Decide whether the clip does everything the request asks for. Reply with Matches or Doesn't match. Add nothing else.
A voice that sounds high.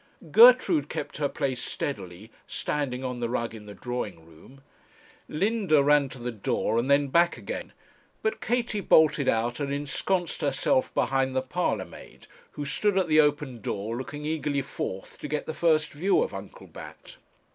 Doesn't match